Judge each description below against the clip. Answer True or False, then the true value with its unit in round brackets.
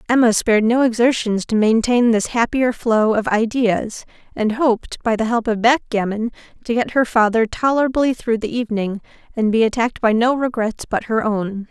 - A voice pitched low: False (230 Hz)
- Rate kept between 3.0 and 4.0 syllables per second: False (5.1 syllables/s)